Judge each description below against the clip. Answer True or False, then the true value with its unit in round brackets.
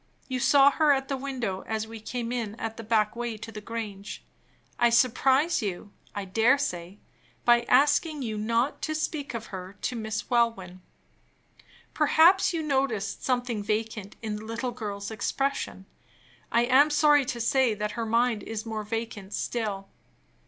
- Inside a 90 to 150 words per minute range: False (165 wpm)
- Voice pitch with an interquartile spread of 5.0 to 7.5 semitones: False (3.8 semitones)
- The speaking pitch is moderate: False (230 Hz)